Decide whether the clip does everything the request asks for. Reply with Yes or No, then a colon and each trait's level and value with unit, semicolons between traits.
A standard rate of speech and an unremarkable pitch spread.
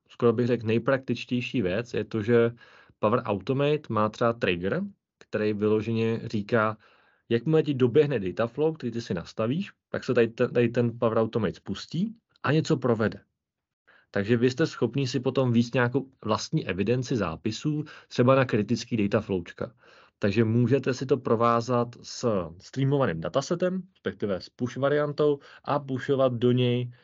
Yes: average, 155 wpm; average, 3.2 semitones